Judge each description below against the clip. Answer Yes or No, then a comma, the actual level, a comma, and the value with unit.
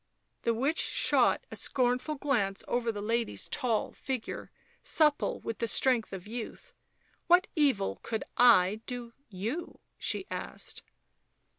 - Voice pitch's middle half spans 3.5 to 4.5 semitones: Yes, average, 3.8 semitones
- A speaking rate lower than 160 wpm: Yes, average, 140 wpm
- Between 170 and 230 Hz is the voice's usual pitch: No, high, 240 Hz